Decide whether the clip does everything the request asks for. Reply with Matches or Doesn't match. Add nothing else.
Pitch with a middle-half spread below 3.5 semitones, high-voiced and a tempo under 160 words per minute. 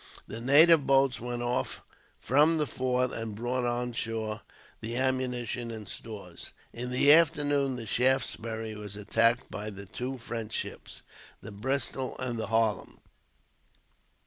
Doesn't match